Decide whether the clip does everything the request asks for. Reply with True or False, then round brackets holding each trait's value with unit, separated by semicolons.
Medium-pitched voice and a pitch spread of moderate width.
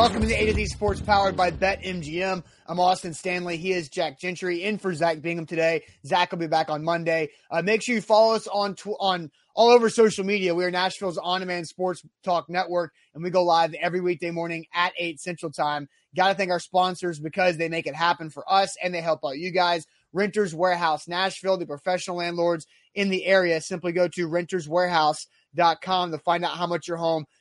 False (175 Hz; 2.0 semitones)